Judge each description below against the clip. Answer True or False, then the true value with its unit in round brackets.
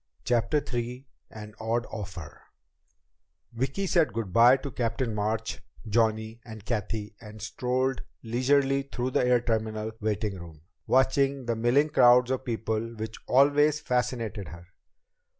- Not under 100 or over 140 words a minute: True (135 wpm)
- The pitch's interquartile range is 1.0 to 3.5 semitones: True (3.0 semitones)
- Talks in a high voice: False (115 Hz)